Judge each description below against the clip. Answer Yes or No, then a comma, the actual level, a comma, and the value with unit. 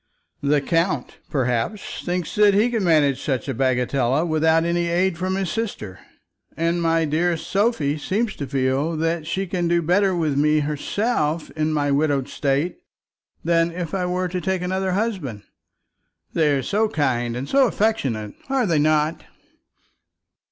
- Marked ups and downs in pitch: No, average, 4.6 semitones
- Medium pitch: Yes, medium, 165 Hz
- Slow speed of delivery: No, average, 160 wpm